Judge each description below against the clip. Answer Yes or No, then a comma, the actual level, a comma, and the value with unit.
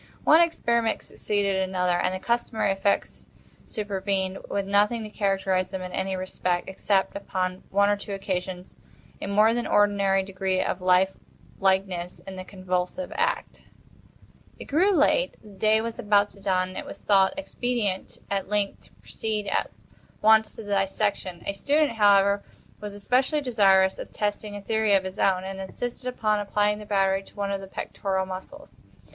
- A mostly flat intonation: Yes, narrow, 2.0 semitones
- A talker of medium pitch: No, high, 200 Hz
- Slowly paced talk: No, average, 170 wpm